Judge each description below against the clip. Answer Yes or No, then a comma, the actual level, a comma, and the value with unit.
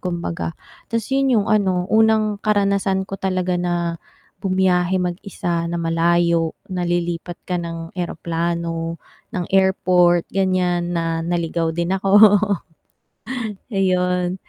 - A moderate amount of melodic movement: No, narrow, 2.1 semitones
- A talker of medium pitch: Yes, medium, 180 Hz